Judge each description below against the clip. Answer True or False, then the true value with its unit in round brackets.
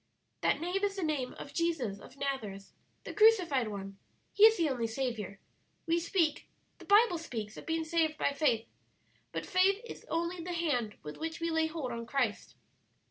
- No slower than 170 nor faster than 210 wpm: True (185 wpm)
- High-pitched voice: True (310 Hz)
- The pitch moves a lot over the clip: True (6.4 semitones)